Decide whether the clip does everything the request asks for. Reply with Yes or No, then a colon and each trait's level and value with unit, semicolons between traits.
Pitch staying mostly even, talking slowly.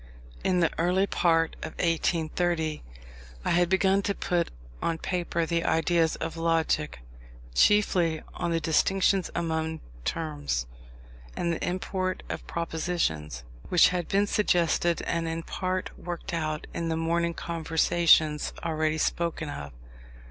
Yes: narrow, 1.7 semitones; slow, 130 wpm